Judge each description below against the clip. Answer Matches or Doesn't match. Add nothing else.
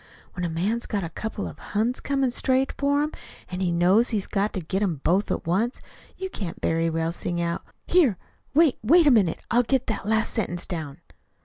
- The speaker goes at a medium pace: Doesn't match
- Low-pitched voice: Doesn't match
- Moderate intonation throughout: Doesn't match